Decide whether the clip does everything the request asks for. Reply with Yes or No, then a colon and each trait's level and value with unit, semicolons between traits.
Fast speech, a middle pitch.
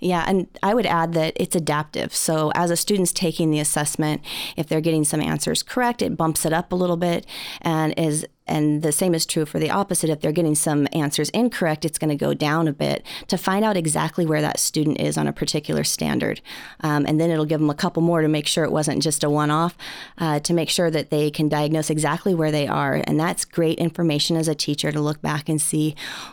Yes: fast, 235 wpm; medium, 160 Hz